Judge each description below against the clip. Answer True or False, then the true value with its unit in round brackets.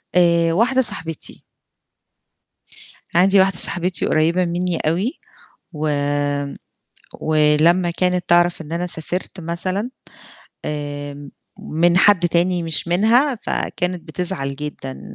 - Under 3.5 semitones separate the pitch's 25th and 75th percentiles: True (2.9 semitones)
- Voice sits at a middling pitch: True (170 Hz)